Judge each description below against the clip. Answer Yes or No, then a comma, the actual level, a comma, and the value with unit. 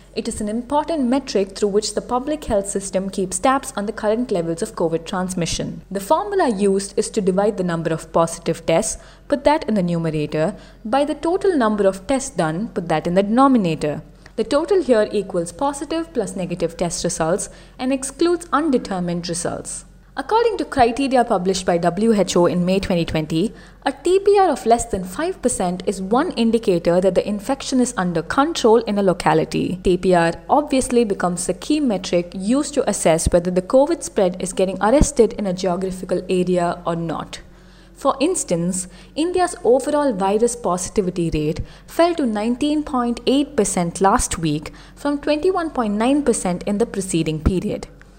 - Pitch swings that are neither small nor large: No, wide, 6.8 semitones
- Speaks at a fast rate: No, average, 160 wpm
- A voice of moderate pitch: No, high, 210 Hz